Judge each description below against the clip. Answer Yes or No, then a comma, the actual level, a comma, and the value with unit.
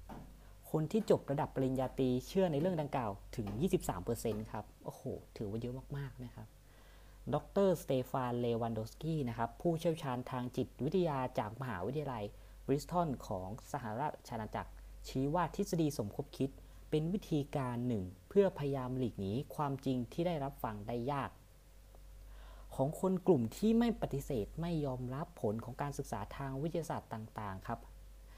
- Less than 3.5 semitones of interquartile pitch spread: No, average, 5.2 semitones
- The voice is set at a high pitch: No, low, 130 Hz